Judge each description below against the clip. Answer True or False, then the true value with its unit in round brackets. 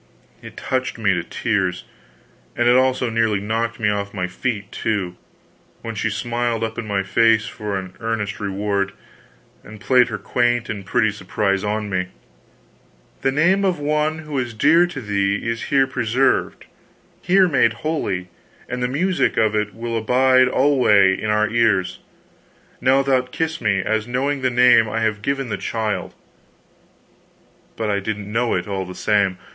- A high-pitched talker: False (115 Hz)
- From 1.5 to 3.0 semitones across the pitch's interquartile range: False (3.7 semitones)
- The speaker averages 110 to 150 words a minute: False (165 wpm)